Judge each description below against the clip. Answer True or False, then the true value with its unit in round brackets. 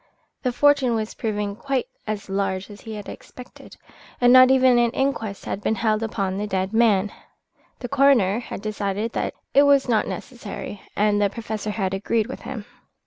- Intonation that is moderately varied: True (3.4 semitones)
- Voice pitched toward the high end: True (220 Hz)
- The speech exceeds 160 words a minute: True (180 wpm)